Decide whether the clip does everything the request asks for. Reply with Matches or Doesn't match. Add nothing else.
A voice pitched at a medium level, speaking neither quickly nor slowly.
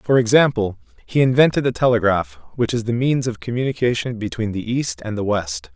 Doesn't match